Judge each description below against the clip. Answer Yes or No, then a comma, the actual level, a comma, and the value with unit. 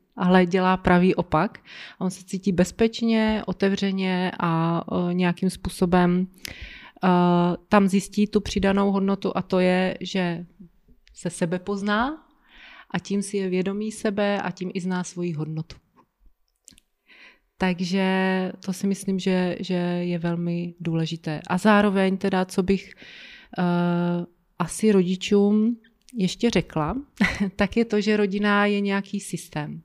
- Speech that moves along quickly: No, average, 125 wpm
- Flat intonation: Yes, narrow, 2.2 semitones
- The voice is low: No, high, 190 Hz